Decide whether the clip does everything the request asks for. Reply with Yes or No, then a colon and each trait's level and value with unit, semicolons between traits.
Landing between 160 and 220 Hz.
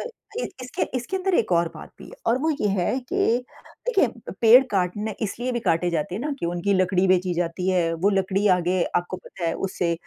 Yes: high, 190 Hz